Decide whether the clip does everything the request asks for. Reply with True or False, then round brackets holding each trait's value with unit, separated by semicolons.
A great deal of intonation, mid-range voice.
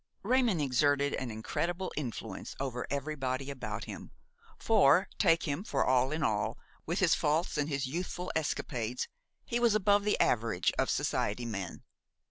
True (5.7 semitones; 145 Hz)